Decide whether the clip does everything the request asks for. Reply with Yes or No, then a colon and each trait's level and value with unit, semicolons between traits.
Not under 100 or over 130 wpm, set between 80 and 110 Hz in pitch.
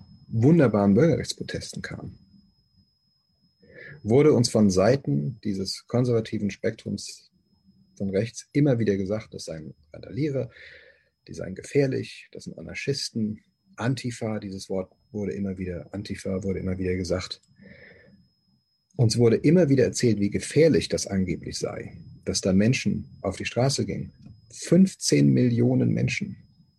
Yes: slow, 125 wpm; low, 105 Hz